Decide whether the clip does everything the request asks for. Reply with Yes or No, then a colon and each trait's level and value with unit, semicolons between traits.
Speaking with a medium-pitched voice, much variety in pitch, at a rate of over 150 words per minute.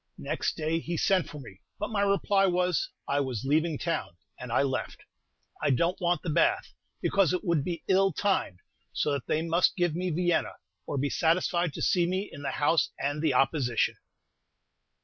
No: medium, 165 Hz; average, 4.2 semitones; average, 190 wpm